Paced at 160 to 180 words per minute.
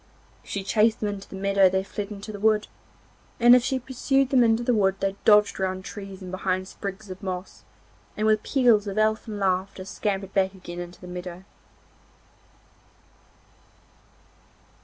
Yes: average, 165 wpm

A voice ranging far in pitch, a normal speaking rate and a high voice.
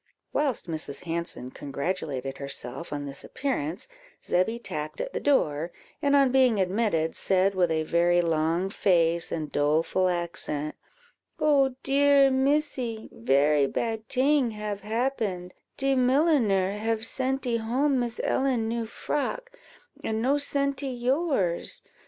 No: wide, 8.0 semitones; slow, 130 wpm; high, 215 Hz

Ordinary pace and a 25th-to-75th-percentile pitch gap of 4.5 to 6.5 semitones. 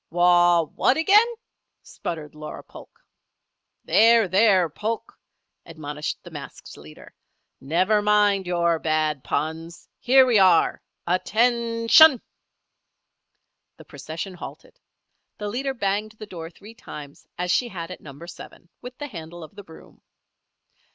No: slow, 125 wpm; wide, 5.5 semitones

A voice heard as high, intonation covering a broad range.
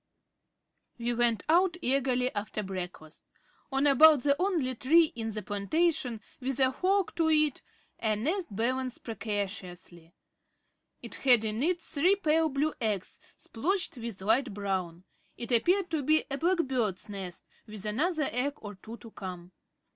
Yes: very high, 250 Hz; wide, 6.7 semitones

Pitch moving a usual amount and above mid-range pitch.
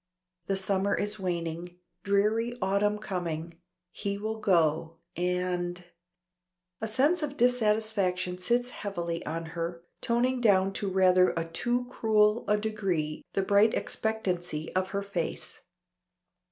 Yes: average, 3.7 semitones; high, 195 Hz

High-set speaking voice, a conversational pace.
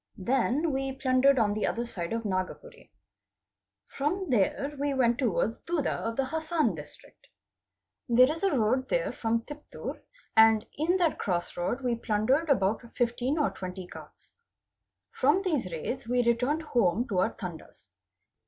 Yes: very high, 250 Hz; average, 155 wpm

